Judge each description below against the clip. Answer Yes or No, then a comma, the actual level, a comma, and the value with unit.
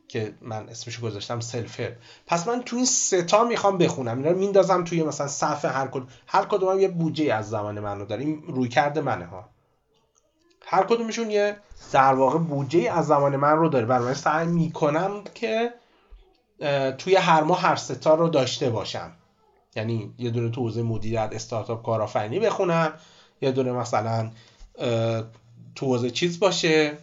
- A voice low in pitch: No, medium, 145 Hz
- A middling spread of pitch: No, wide, 6.8 semitones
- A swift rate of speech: Yes, fast, 165 wpm